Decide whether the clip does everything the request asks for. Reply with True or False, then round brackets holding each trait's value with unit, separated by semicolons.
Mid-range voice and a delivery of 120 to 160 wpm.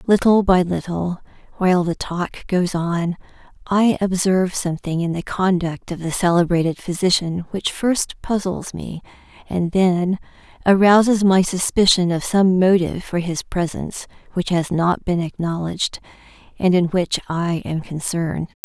True (180 Hz; 140 wpm)